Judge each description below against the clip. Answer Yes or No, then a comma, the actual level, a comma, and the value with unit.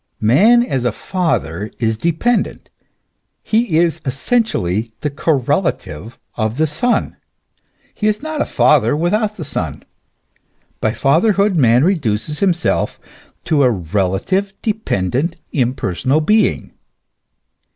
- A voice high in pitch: No, medium, 155 Hz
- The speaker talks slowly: Yes, slow, 110 wpm